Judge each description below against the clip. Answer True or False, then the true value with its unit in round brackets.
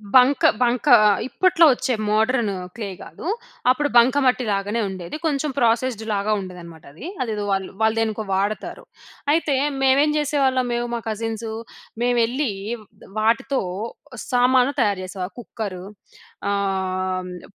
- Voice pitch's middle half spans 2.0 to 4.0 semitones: False (4.5 semitones)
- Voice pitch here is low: False (230 Hz)